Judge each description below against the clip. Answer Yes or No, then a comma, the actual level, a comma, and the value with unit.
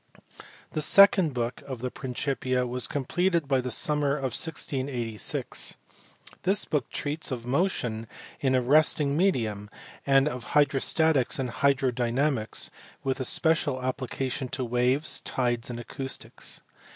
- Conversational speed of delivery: No, slow, 125 wpm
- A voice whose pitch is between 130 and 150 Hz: Yes, low, 135 Hz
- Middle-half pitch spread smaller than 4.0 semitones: Yes, average, 3.1 semitones